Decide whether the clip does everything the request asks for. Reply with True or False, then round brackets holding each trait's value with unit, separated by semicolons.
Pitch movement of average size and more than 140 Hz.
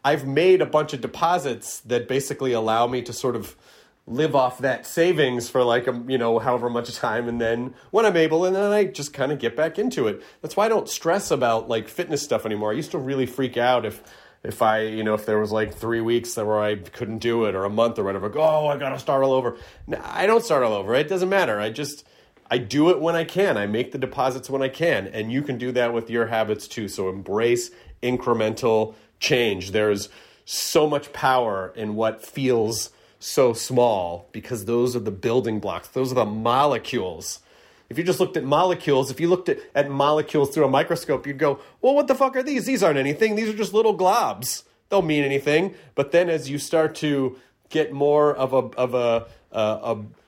False (4.6 semitones; 130 Hz)